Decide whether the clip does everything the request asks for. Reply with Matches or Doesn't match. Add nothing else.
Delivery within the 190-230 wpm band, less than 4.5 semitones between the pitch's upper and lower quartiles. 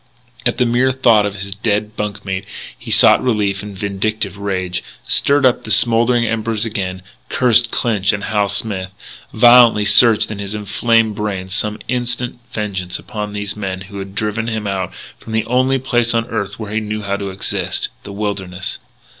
Doesn't match